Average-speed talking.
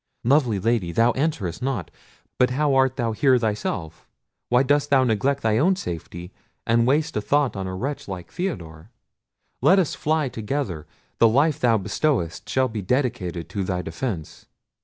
Yes: average, 165 wpm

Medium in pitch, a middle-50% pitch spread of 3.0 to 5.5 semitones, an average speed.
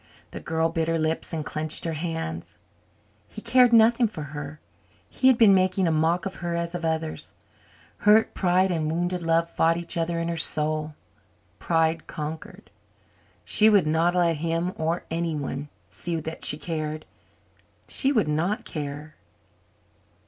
No: medium, 165 Hz; narrow, 2.4 semitones; average, 155 wpm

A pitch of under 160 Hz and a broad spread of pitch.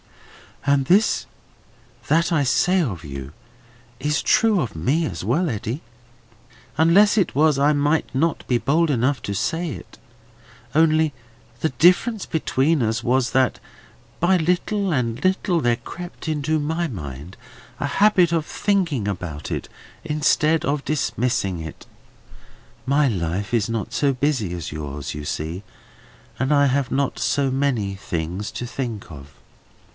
Yes: medium, 140 Hz; wide, 7.5 semitones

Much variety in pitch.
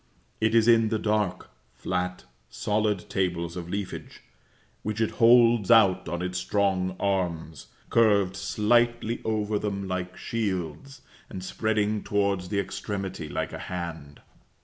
No: average, 3.1 semitones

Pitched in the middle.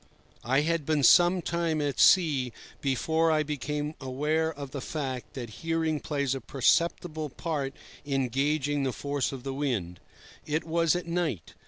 Yes: medium, 145 Hz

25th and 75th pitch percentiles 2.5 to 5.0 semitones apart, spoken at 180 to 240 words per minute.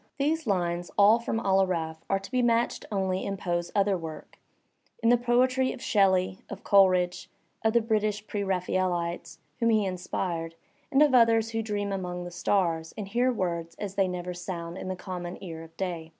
Yes: average, 3.9 semitones; average, 190 wpm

